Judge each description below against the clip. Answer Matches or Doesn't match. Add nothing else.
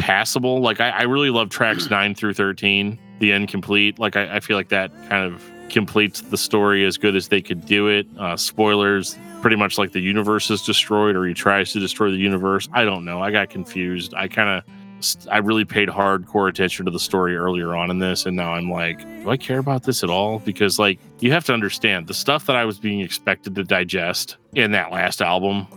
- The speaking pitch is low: Matches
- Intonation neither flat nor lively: Doesn't match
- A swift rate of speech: Matches